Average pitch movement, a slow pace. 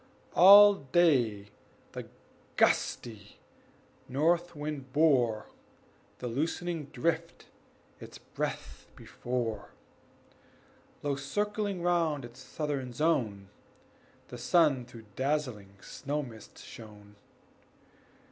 No: wide, 5.7 semitones; slow, 85 wpm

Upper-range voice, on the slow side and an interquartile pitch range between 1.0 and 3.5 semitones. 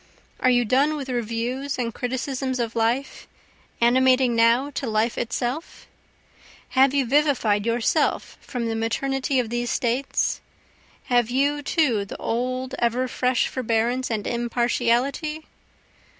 Yes: very high, 250 Hz; slow, 125 wpm; narrow, 2.4 semitones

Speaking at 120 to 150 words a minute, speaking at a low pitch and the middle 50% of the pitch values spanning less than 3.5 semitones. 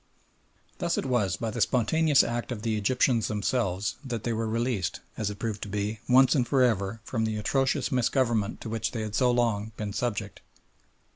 No: average, 195 wpm; low, 115 Hz; average, 3.0 semitones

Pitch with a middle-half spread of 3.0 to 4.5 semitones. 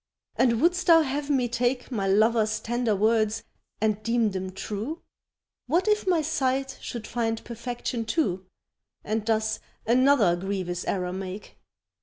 Yes: average, 4.0 semitones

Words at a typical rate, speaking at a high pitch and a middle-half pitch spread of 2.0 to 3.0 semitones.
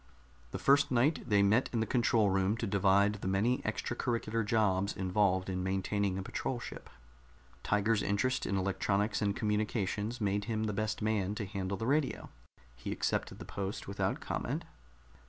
No: average, 165 wpm; low, 105 Hz; narrow, 2.5 semitones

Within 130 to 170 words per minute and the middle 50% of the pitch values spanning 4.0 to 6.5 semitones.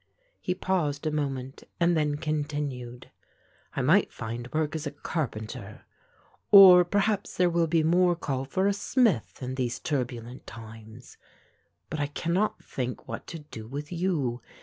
Yes: average, 150 wpm; wide, 5.5 semitones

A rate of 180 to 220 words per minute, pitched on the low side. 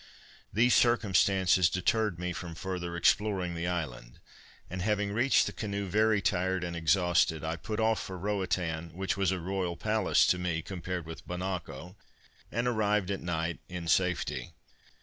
No: average, 155 wpm; very low, 90 Hz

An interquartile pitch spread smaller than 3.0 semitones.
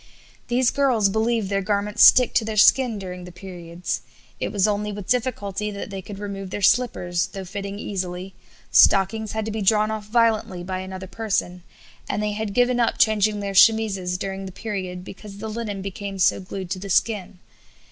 Yes: narrow, 2.5 semitones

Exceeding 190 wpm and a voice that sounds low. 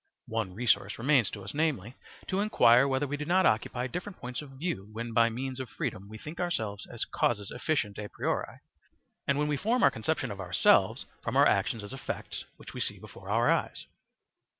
Yes: average, 200 wpm; low, 125 Hz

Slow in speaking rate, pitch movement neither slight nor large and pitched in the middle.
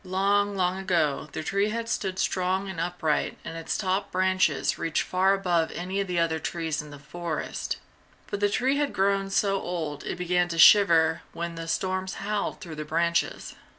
No: average, 185 wpm; average, 3.0 semitones; medium, 180 Hz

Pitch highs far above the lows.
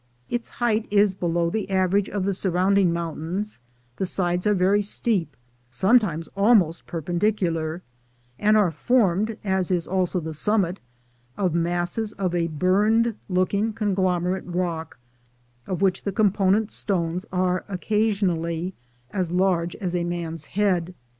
No: average, 3.0 semitones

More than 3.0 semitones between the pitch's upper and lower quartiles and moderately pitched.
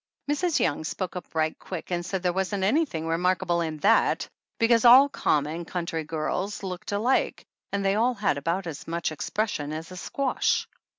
Yes: average, 4.3 semitones; medium, 180 Hz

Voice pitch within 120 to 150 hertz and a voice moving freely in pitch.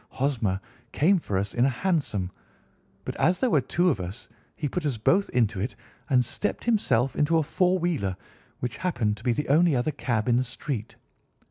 Yes: low, 135 Hz; wide, 6.7 semitones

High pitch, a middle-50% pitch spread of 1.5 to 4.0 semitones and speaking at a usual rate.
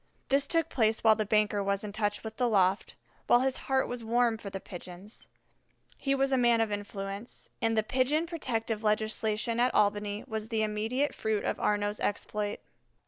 Yes: high, 220 Hz; average, 2.8 semitones; average, 185 wpm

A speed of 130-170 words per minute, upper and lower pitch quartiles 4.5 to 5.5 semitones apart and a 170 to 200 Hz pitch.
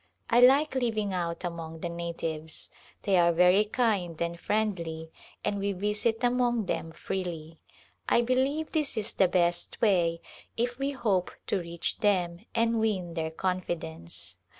Yes: average, 150 wpm; average, 5.1 semitones; medium, 185 Hz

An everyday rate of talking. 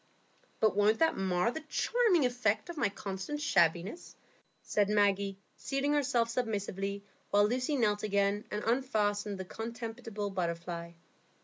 No: slow, 130 wpm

